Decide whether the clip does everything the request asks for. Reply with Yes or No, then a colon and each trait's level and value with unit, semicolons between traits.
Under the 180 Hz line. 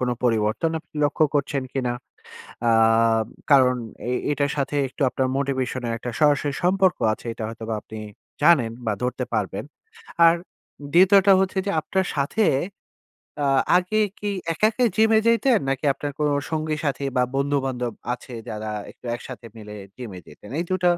Yes: medium, 140 Hz